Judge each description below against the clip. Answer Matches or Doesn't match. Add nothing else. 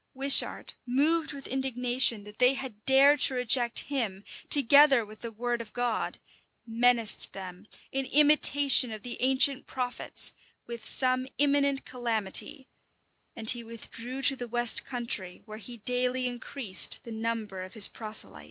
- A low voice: Doesn't match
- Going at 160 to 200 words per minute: Doesn't match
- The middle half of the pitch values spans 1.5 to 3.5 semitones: Matches